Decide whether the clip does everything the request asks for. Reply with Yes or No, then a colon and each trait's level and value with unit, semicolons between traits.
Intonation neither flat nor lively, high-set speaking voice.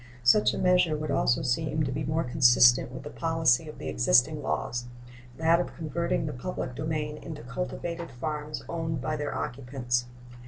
No: average, 4.6 semitones; medium, 150 Hz